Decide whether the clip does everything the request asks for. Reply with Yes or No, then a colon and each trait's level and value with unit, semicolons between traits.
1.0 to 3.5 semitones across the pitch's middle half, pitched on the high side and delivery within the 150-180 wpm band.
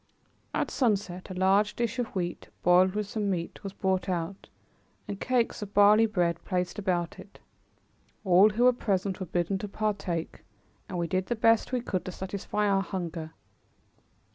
Yes: narrow, 2.6 semitones; high, 195 Hz; average, 170 wpm